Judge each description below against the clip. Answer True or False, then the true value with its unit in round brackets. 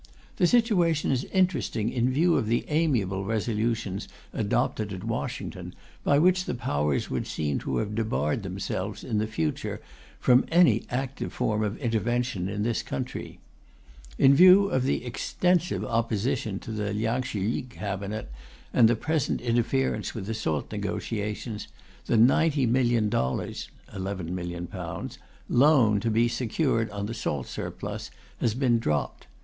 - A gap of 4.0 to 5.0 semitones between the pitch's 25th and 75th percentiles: True (4.3 semitones)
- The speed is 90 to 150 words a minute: True (140 wpm)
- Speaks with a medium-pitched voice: False (115 Hz)